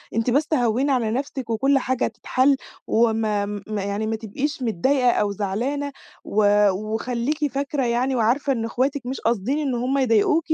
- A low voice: No, high, 240 Hz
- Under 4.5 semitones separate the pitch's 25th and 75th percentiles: Yes, average, 3.9 semitones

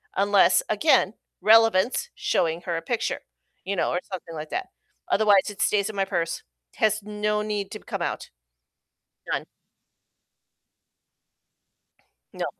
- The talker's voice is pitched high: Yes, high, 205 Hz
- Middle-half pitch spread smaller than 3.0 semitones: Yes, narrow, 2.4 semitones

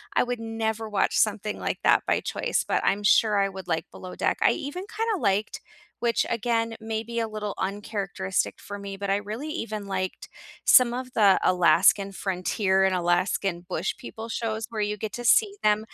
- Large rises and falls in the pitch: No, average, 2.7 semitones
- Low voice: No, high, 210 Hz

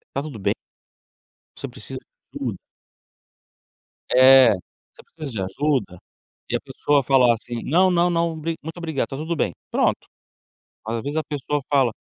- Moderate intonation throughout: Yes, average, 4.1 semitones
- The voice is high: No, medium, 145 Hz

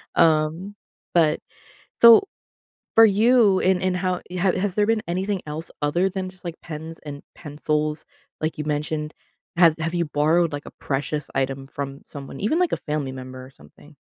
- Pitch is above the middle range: No, medium, 160 Hz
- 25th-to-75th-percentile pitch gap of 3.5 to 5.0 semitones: Yes, average, 4.0 semitones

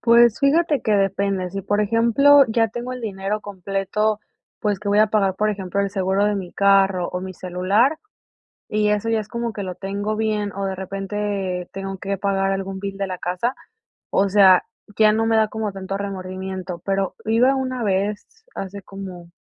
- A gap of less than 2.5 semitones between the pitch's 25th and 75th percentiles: Yes, narrow, 2.1 semitones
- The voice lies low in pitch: No, high, 200 Hz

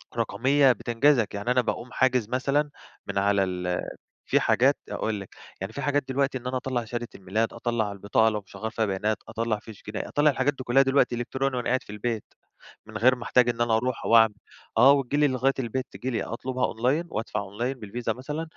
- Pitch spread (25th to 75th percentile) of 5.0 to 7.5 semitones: No, average, 3.3 semitones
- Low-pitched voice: Yes, low, 120 Hz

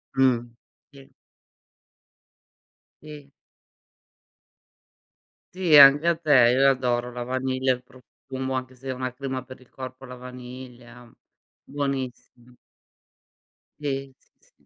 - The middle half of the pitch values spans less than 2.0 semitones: Yes, narrow, 1.5 semitones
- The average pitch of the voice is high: No, low, 130 Hz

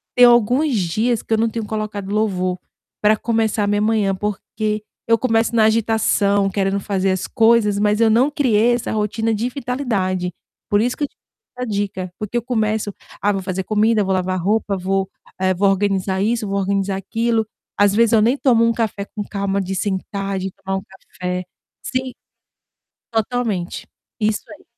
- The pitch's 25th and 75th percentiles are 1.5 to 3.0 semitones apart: Yes, average, 2.7 semitones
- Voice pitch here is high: Yes, high, 210 Hz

